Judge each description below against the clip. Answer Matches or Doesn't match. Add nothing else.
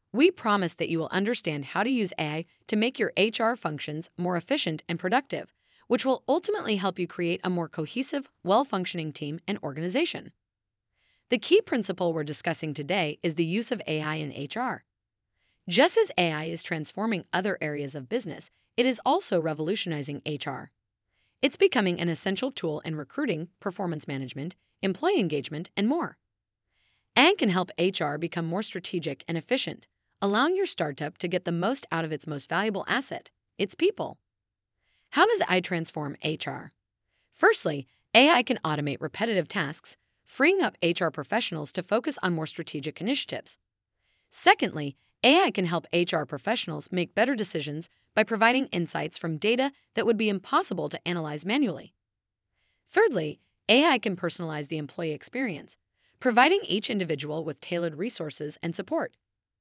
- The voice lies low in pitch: Doesn't match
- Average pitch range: Doesn't match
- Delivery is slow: Doesn't match